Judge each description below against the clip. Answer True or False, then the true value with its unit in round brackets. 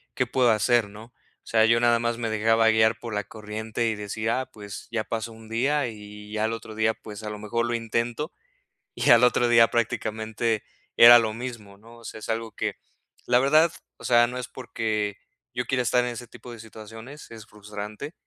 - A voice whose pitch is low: True (115 Hz)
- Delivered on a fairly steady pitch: True (1.7 semitones)